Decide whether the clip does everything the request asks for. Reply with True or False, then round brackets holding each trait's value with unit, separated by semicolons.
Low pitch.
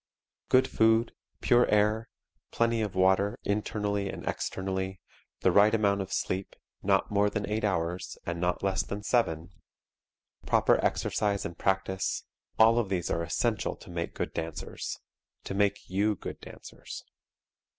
True (100 Hz)